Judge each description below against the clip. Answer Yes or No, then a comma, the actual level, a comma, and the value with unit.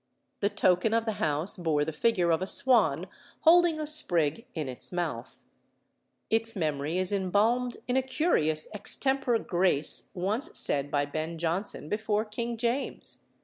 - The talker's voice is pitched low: No, high, 195 Hz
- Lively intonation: Yes, wide, 6.7 semitones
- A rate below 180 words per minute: Yes, average, 150 wpm